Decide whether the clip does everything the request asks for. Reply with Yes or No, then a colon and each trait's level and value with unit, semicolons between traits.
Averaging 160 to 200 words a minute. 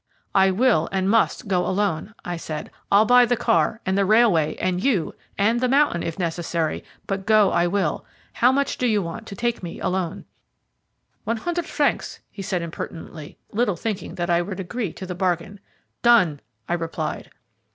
Yes: average, 180 wpm